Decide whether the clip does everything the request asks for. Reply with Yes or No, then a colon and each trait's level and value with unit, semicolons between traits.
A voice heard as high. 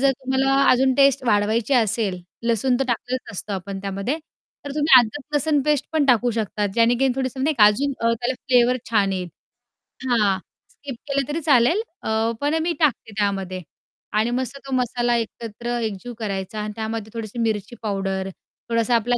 Yes: high, 235 Hz